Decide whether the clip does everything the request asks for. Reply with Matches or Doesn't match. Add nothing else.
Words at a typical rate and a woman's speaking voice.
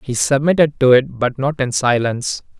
Doesn't match